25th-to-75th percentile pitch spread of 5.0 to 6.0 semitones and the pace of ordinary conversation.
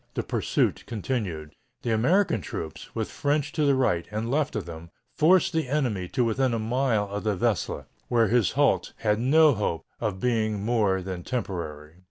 Yes: wide, 5.5 semitones; average, 180 wpm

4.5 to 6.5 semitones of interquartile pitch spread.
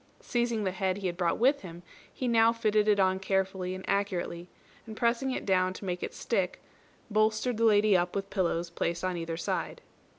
No: average, 3.1 semitones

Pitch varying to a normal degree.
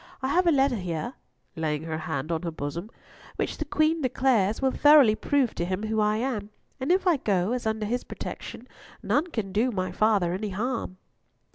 No: wide, 6.2 semitones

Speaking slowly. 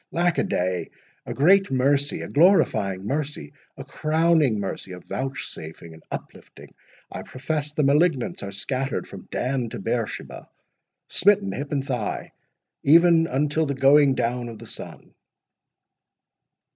Yes: slow, 115 wpm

